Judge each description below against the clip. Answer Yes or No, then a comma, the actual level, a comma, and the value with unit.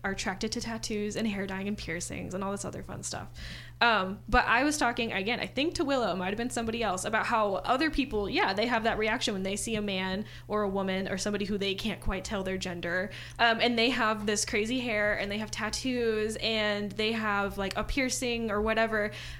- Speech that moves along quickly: Yes, fast, 235 wpm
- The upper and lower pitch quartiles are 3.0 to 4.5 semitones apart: No, narrow, 2.6 semitones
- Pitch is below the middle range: No, high, 215 Hz